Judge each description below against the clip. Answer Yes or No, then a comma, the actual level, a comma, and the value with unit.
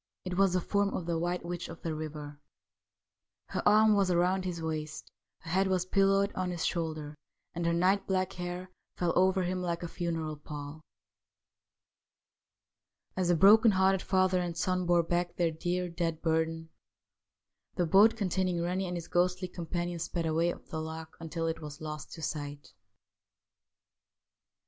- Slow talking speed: No, average, 170 wpm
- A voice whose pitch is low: No, medium, 175 Hz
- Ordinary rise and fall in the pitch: No, narrow, 2.3 semitones